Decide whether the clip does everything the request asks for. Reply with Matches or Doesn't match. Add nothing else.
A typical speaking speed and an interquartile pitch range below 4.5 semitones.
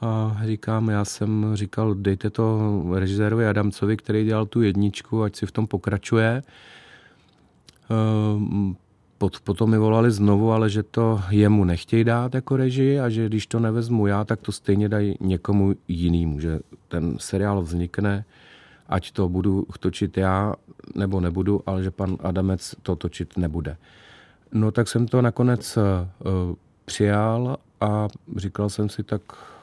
Matches